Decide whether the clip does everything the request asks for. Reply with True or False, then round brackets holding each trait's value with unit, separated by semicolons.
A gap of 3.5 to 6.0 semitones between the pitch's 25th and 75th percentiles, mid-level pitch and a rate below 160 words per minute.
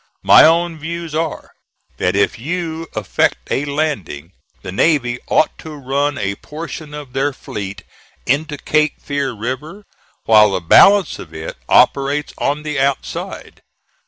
True (5.1 semitones; 145 Hz; 140 wpm)